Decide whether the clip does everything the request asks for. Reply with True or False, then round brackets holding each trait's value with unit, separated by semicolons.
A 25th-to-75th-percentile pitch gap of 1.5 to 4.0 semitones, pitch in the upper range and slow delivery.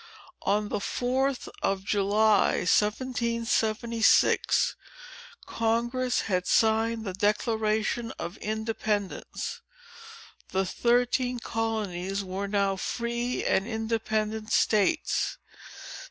True (2.5 semitones; 220 Hz; 80 wpm)